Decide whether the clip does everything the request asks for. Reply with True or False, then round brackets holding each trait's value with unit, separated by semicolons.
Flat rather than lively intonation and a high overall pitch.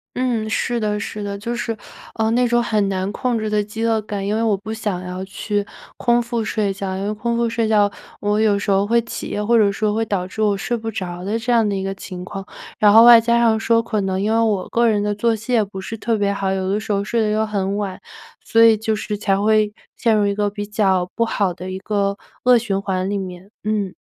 True (2.2 semitones; 210 Hz)